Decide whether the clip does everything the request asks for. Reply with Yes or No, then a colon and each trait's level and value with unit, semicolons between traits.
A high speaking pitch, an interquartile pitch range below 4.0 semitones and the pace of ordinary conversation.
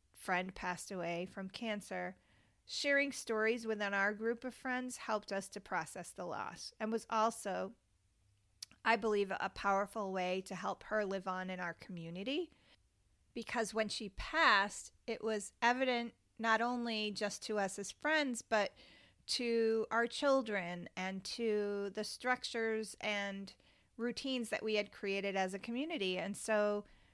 Yes: high, 210 Hz; average, 3.2 semitones; average, 150 wpm